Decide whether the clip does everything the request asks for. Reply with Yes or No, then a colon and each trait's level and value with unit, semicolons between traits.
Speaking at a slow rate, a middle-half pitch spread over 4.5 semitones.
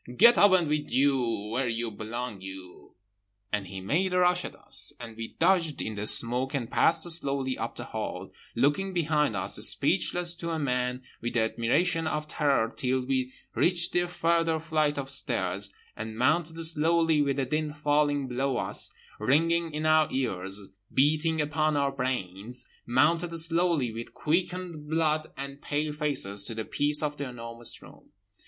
No: average, 160 wpm; average, 5.1 semitones